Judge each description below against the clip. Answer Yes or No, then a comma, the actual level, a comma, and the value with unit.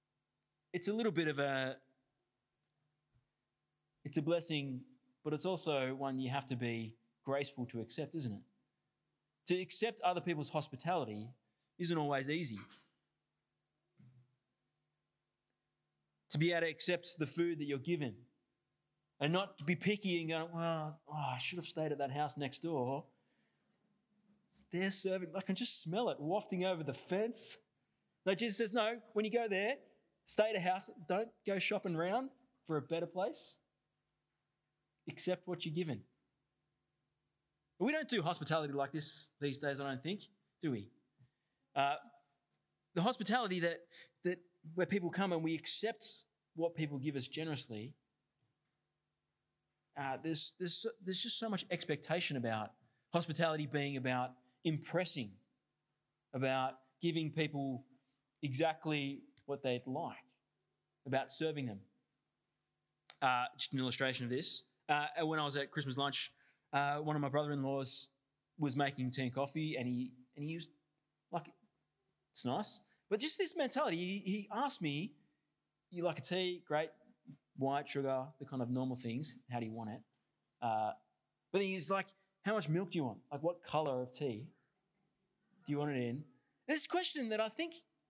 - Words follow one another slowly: No, average, 155 wpm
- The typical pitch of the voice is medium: Yes, medium, 150 Hz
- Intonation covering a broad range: No, average, 4.9 semitones